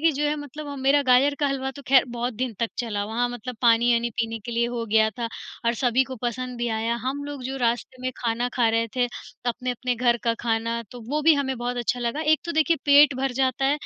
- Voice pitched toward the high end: Yes, very high, 250 Hz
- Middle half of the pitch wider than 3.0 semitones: No, narrow, 2.6 semitones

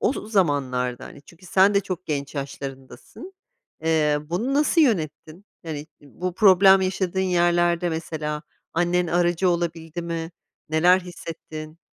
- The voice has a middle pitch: Yes, medium, 170 Hz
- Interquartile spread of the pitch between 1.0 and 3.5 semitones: Yes, average, 3.2 semitones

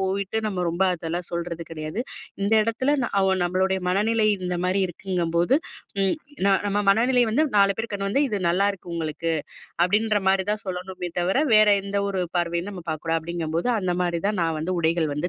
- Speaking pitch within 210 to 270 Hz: No, medium, 185 Hz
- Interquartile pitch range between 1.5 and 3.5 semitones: Yes, average, 3.0 semitones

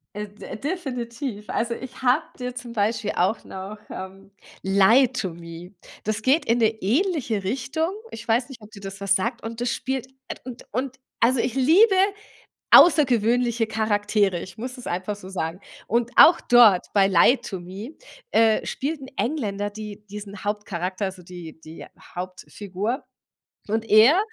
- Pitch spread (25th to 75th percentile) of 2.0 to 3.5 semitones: No, average, 4.2 semitones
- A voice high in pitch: Yes, high, 220 Hz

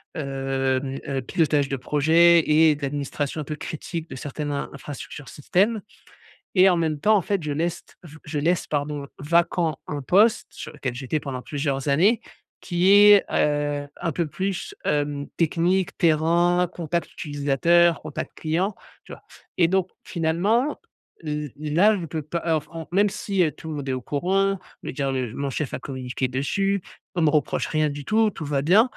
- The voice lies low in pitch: No, medium, 155 Hz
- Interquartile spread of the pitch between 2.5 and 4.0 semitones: Yes, average, 3.7 semitones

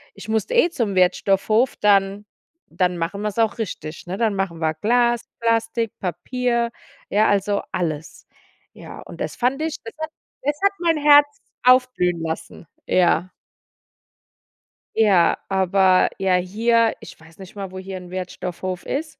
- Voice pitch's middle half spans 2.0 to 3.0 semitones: No, average, 4.6 semitones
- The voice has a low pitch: No, high, 200 Hz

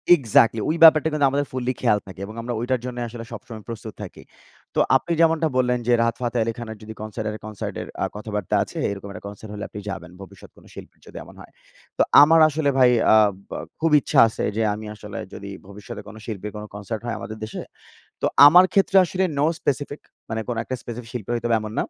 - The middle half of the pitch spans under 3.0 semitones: No, average, 3.6 semitones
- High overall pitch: No, low, 115 Hz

